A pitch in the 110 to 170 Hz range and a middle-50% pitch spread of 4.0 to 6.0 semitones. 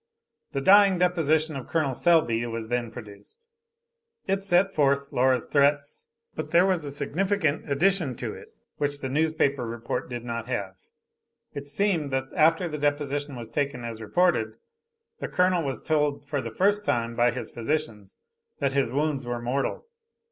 Yes: medium, 140 Hz; average, 5.0 semitones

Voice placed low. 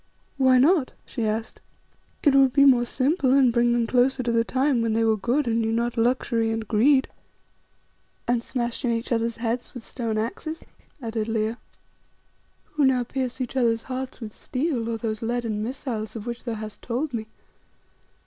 No: high, 240 Hz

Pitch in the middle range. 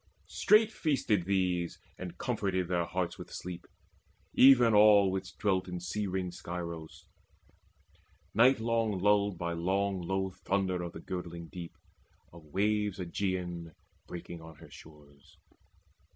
No: very low, 95 Hz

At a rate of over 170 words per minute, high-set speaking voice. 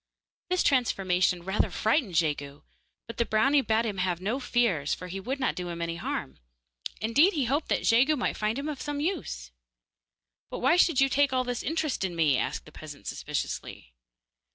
Yes: average, 190 wpm; high, 230 Hz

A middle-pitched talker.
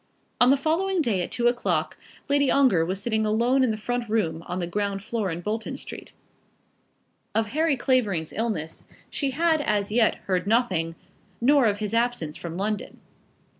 No: high, 220 Hz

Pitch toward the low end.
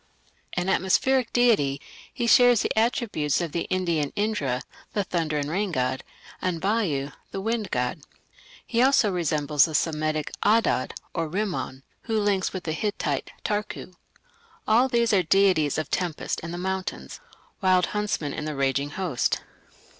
No: medium, 180 Hz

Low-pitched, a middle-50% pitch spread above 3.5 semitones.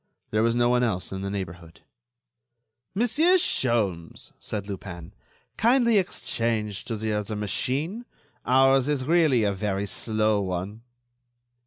Yes: low, 110 Hz; average, 5.2 semitones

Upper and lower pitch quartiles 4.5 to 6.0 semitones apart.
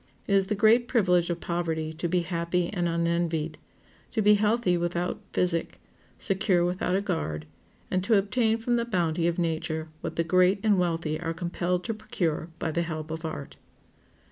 No: average, 3.1 semitones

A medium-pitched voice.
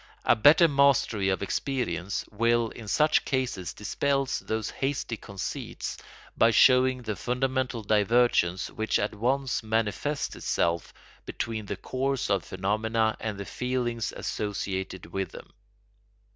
No: low, 115 Hz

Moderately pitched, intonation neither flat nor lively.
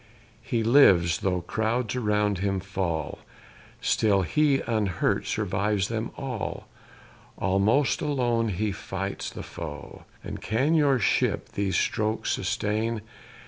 No: low, 105 Hz; average, 3.4 semitones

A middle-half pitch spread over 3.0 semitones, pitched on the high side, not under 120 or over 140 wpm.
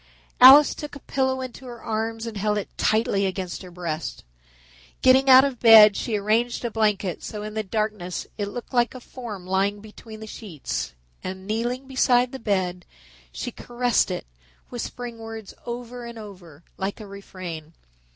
No: average, 3.7 semitones; high, 220 Hz; average, 170 wpm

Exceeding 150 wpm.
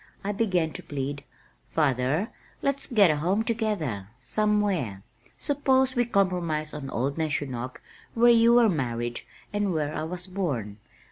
No: average, 140 wpm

